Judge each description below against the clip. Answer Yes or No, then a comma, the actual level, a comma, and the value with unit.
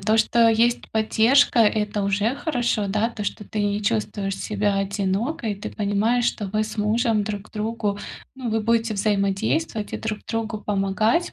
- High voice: Yes, high, 215 Hz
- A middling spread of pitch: No, narrow, 2.0 semitones